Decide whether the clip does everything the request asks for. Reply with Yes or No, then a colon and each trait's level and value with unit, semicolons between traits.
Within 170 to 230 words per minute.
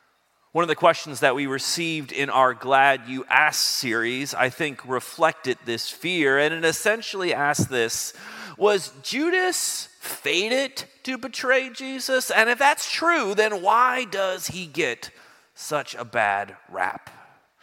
No: average, 145 wpm